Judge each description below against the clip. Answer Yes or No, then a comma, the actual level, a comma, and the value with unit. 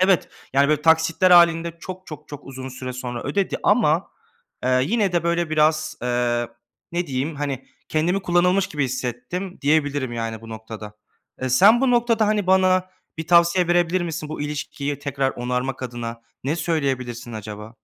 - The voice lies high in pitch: No, medium, 150 Hz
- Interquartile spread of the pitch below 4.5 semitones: No, wide, 5.5 semitones